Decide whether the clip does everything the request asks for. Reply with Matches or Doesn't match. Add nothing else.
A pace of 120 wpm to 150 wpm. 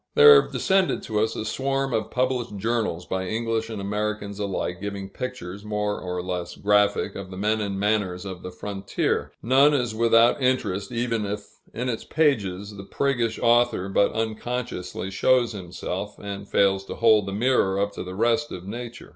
Doesn't match